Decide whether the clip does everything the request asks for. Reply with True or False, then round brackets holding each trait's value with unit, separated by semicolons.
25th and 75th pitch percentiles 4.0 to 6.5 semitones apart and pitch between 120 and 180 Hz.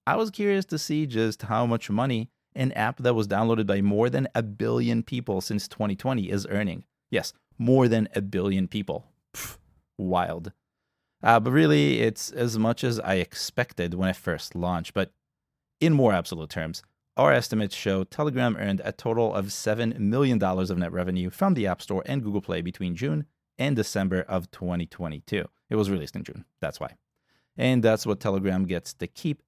False (4.6 semitones; 105 Hz)